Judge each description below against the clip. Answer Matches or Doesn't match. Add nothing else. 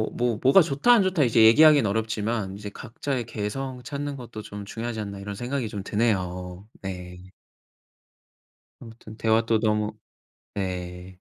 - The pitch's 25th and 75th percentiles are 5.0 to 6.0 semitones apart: Doesn't match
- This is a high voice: Doesn't match